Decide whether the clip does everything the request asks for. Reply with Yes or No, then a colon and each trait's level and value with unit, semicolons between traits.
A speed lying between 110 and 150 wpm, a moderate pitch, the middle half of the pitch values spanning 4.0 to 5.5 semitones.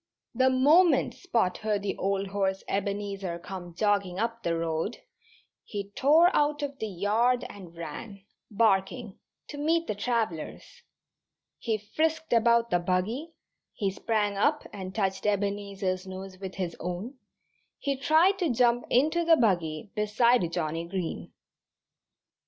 No: slow, 135 wpm; high, 205 Hz; average, 4.8 semitones